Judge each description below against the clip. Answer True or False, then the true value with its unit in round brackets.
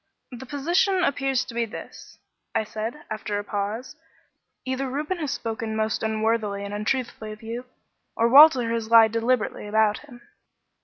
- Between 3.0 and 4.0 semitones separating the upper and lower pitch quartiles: True (3.3 semitones)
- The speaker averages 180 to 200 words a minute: False (155 wpm)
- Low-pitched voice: False (230 Hz)